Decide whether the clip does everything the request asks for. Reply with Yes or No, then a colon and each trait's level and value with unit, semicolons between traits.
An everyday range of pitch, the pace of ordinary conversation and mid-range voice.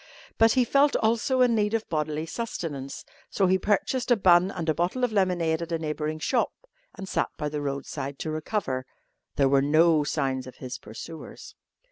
No: wide, 6.0 semitones; average, 185 wpm; medium, 165 Hz